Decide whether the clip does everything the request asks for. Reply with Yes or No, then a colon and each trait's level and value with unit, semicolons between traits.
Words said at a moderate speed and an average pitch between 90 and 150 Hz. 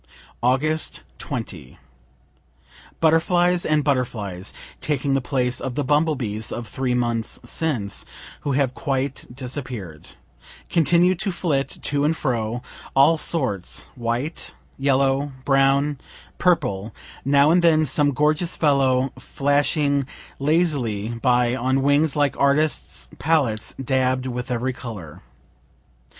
No: slow, 115 wpm; low, 135 Hz